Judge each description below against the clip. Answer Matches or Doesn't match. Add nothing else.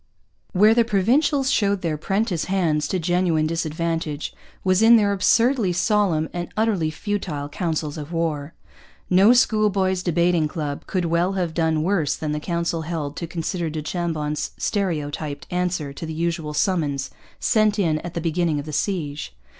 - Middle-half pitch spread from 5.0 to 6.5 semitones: Doesn't match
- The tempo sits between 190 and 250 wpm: Doesn't match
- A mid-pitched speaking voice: Matches